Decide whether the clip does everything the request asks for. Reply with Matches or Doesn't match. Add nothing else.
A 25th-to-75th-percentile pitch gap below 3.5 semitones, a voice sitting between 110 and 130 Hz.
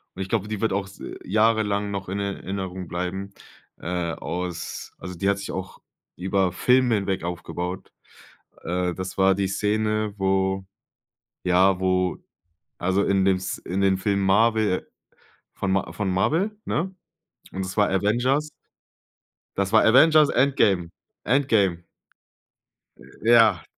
Doesn't match